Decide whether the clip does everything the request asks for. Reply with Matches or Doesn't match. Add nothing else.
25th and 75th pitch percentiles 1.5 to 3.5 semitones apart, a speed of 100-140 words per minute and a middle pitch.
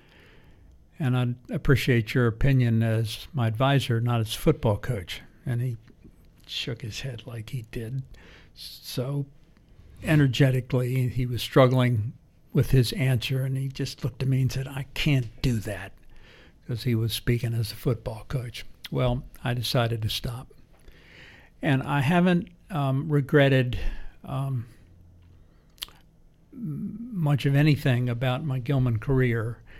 Doesn't match